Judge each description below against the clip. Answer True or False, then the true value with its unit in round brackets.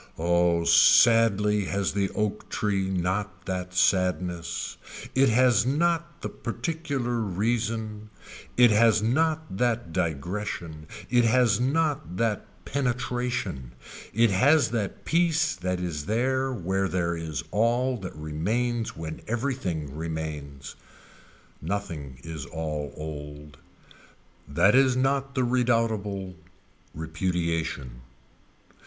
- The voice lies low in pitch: True (100 Hz)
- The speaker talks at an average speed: False (105 wpm)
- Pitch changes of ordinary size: False (6.5 semitones)